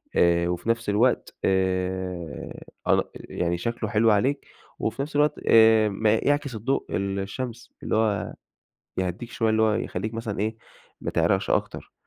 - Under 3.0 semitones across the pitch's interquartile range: No, average, 3.6 semitones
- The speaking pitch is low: Yes, low, 110 Hz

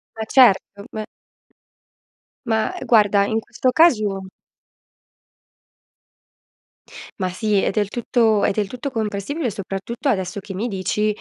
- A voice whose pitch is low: No, high, 215 Hz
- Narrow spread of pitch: No, average, 3.0 semitones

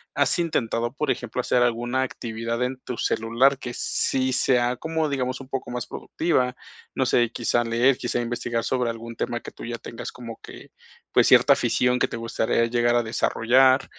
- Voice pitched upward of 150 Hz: No, low, 120 Hz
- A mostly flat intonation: Yes, narrow, 1.8 semitones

